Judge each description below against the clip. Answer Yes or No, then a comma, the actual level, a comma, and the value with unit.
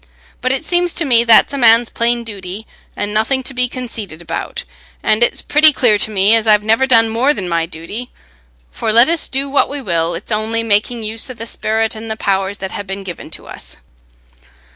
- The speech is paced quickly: Yes, fast, 215 wpm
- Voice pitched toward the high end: Yes, high, 225 Hz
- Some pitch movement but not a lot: Yes, average, 3.5 semitones